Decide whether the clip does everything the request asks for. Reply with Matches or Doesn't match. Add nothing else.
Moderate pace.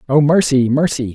Matches